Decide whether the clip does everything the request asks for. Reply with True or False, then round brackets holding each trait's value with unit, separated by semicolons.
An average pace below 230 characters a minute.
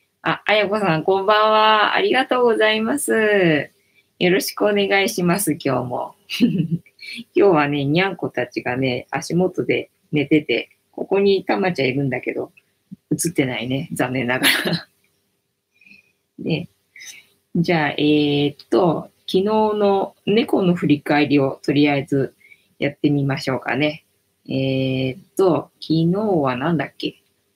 False (265 characters per minute)